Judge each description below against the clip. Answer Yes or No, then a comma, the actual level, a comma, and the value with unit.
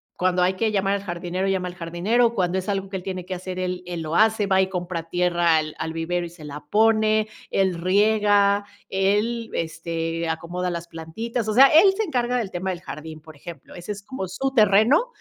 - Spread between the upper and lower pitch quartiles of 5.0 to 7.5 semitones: No, average, 3.7 semitones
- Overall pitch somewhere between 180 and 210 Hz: Yes, medium, 185 Hz